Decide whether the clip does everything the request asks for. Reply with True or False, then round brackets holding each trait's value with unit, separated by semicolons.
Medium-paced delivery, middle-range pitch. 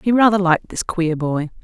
False (220 wpm; 180 Hz)